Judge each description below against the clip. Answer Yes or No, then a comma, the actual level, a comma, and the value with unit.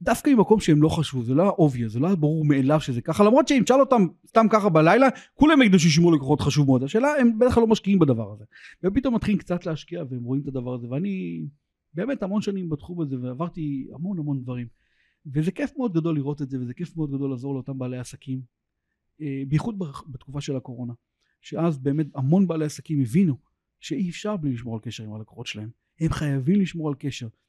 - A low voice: No, medium, 150 Hz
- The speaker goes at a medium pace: No, fast, 195 wpm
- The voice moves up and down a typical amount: No, wide, 6.3 semitones